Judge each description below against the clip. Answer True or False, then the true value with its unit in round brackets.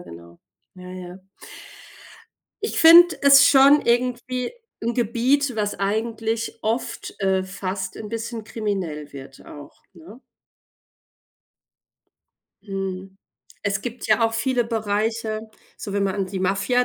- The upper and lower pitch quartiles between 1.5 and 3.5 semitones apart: False (3.9 semitones)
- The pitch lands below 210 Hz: False (215 Hz)